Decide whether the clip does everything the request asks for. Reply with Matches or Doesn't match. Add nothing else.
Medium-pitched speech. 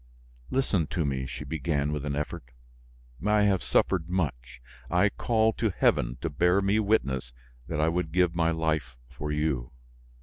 Doesn't match